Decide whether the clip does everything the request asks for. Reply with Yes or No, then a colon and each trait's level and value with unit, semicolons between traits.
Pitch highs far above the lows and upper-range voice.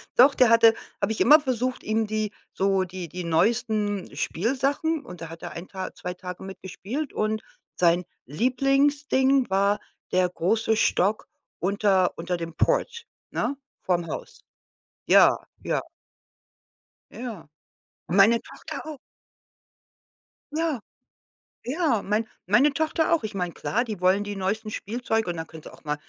Yes: wide, 5.8 semitones; high, 215 Hz